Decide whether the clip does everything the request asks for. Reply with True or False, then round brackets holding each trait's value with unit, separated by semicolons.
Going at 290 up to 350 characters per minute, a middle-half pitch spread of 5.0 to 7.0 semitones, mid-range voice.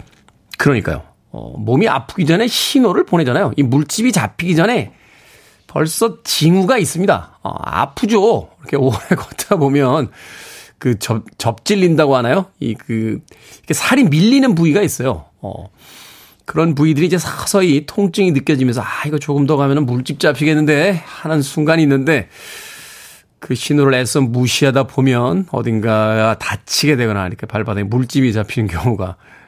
True (320 characters per minute; 5.4 semitones; 145 Hz)